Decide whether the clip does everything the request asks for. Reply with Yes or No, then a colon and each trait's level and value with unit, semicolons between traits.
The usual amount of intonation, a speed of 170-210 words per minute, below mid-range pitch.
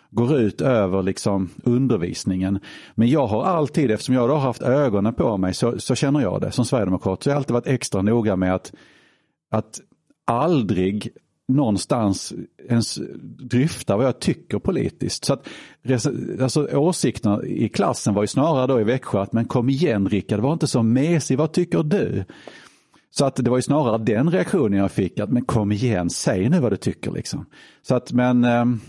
Yes: average, 4.7 semitones; average, 185 wpm; low, 120 Hz